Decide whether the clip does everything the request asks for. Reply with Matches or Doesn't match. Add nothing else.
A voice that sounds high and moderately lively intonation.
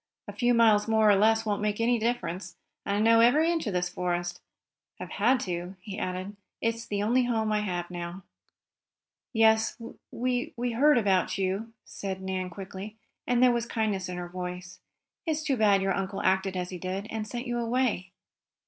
Matches